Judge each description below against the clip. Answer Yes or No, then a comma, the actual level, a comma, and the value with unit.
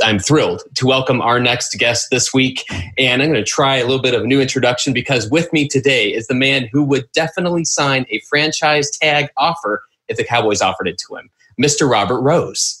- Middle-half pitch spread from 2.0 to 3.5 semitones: Yes, average, 2.9 semitones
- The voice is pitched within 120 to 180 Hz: Yes, low, 135 Hz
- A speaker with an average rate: No, fast, 215 wpm